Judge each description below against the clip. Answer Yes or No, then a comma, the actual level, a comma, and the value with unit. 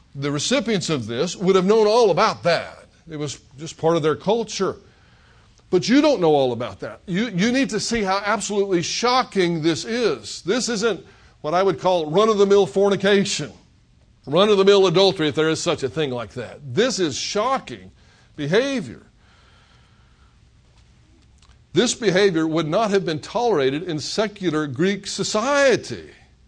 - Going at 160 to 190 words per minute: Yes, average, 165 wpm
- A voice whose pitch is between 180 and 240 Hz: Yes, high, 190 Hz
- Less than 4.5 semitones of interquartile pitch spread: No, average, 5.0 semitones